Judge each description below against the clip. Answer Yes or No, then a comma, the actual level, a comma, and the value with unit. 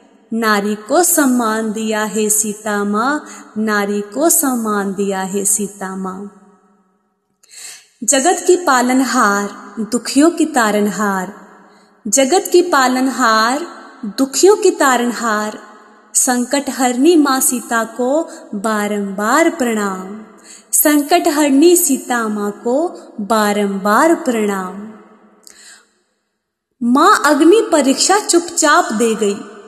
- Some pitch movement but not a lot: No, wide, 5.7 semitones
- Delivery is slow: Yes, slow, 95 wpm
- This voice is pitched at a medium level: No, high, 235 Hz